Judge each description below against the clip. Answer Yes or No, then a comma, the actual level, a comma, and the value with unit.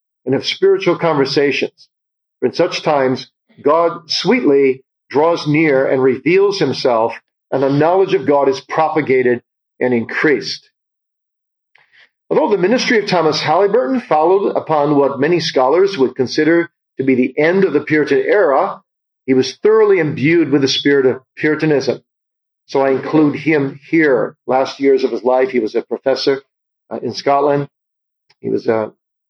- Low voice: No, medium, 145 Hz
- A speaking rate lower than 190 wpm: Yes, average, 155 wpm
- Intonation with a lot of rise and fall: No, average, 4.1 semitones